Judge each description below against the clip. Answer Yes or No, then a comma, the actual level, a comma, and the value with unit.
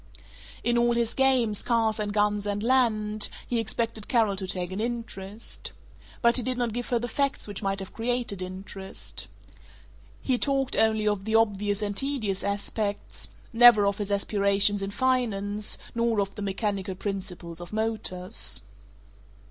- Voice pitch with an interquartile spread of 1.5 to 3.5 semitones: Yes, average, 2.9 semitones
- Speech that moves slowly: No, average, 155 wpm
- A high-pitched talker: Yes, high, 210 Hz